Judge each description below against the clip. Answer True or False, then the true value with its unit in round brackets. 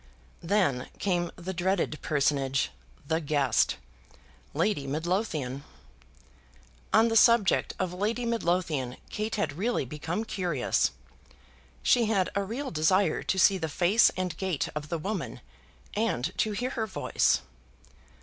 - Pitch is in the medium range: True (180 Hz)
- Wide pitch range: True (5.7 semitones)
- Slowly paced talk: True (130 wpm)